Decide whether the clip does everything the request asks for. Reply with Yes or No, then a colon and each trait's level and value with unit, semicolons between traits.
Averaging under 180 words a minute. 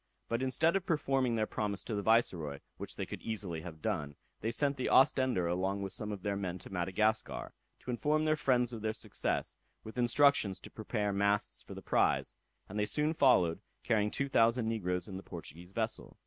No: average, 200 wpm